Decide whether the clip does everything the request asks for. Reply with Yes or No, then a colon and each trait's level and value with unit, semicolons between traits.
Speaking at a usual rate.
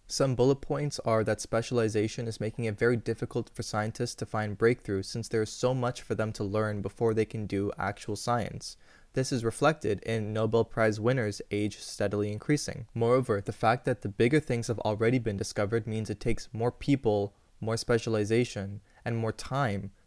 Yes: average, 185 wpm